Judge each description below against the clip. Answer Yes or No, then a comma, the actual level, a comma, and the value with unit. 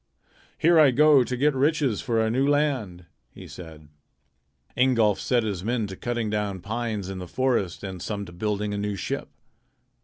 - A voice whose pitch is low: Yes, low, 110 Hz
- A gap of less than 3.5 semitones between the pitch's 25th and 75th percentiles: No, average, 4.7 semitones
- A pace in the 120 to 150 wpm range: No, average, 180 wpm